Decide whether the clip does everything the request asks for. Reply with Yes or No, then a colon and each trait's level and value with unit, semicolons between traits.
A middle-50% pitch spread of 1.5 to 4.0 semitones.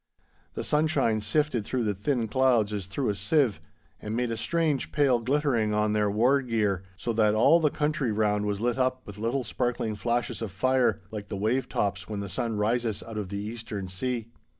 Yes: average, 3.6 semitones